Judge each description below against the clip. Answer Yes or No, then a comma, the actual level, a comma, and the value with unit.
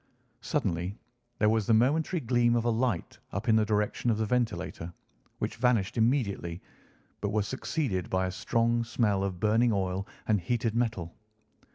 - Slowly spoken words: No, average, 165 wpm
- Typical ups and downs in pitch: Yes, average, 3.5 semitones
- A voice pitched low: Yes, low, 110 Hz